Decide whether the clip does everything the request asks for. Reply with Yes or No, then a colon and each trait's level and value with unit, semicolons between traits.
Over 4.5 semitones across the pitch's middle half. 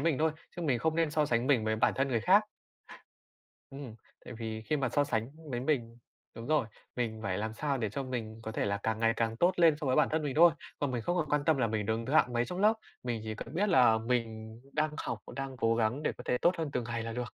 Yes: average, 5.0 semitones